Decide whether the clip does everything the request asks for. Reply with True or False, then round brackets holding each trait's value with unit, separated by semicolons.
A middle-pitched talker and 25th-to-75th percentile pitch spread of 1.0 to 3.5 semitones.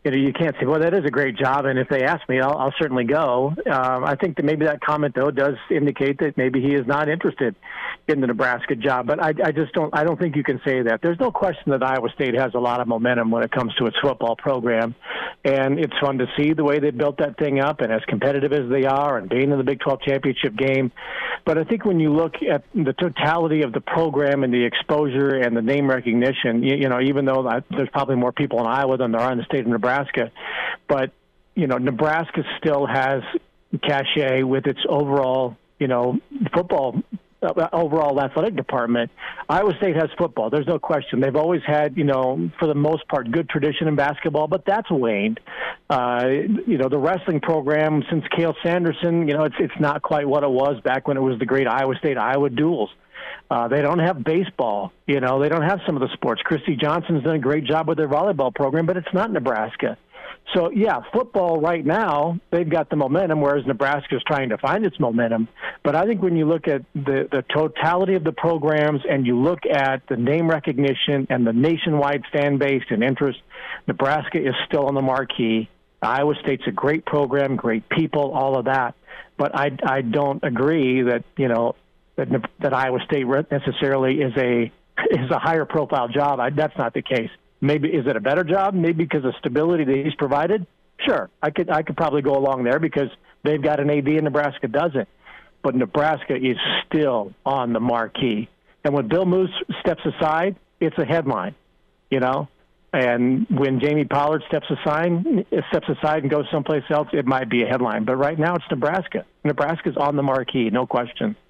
True (145 Hz; 3.1 semitones)